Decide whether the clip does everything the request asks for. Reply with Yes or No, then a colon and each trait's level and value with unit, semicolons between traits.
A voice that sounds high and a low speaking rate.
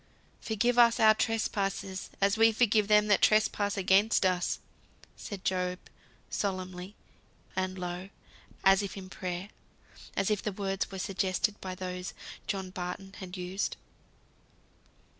Yes: high, 195 Hz; slow, 130 wpm